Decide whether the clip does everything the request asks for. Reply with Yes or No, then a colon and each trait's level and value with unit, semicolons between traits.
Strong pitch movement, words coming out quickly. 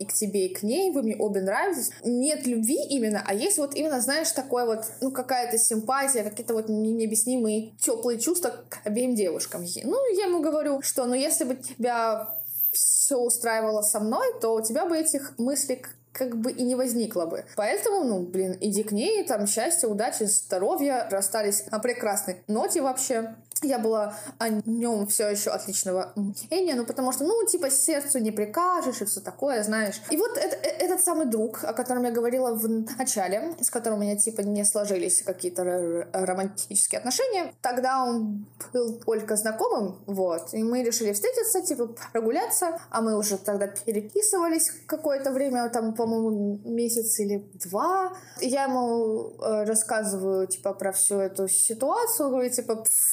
No: average, 4.6 semitones; fast, 170 wpm